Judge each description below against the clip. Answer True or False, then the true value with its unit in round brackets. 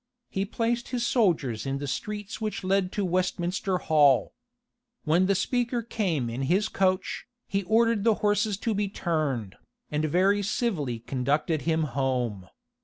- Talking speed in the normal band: True (150 wpm)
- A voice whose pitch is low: False (185 Hz)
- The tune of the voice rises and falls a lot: True (6.4 semitones)